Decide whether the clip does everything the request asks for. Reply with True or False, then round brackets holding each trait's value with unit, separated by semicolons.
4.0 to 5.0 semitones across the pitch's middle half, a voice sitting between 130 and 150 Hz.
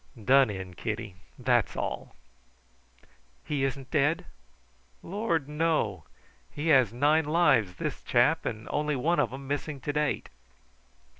True (4.3 semitones; 140 Hz)